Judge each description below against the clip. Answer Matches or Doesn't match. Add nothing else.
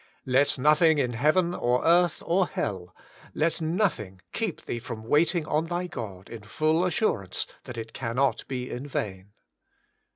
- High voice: Doesn't match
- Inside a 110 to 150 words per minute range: Doesn't match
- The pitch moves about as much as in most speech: Doesn't match